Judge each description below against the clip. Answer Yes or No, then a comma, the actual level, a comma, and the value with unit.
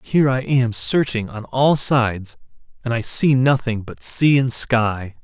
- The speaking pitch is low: Yes, low, 120 Hz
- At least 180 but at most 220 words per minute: No, average, 170 wpm